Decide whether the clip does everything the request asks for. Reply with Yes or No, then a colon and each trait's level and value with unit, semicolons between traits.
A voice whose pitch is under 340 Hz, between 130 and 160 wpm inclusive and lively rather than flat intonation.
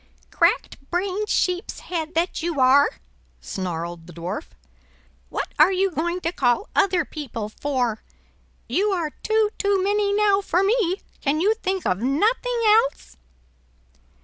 No: very high, 355 Hz; average, 140 wpm; wide, 6.7 semitones